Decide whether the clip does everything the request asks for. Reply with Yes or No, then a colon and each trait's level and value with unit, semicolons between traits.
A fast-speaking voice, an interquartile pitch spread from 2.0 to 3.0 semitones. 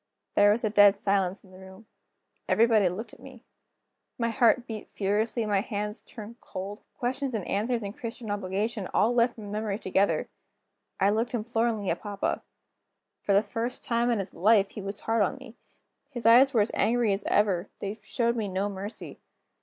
No: average, 185 wpm; average, 2.7 semitones